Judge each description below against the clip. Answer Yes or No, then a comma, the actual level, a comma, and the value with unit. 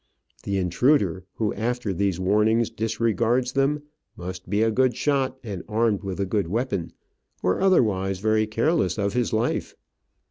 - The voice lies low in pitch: Yes, low, 110 Hz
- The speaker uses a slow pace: No, average, 150 wpm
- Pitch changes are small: No, average, 4.1 semitones